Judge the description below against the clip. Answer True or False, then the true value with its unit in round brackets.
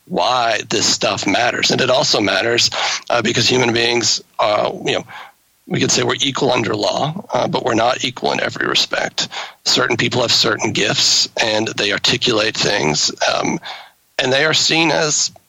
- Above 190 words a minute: False (175 wpm)